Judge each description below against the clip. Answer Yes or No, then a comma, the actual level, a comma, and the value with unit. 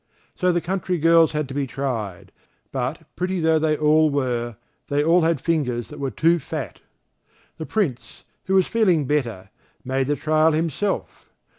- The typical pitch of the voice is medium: Yes, medium, 155 Hz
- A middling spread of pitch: Yes, average, 3.8 semitones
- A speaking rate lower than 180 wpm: Yes, average, 165 wpm